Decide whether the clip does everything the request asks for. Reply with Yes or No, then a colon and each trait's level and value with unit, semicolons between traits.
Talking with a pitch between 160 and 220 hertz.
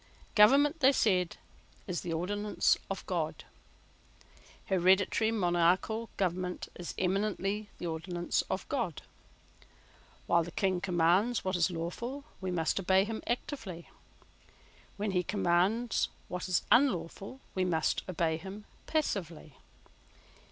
Yes: high, 190 Hz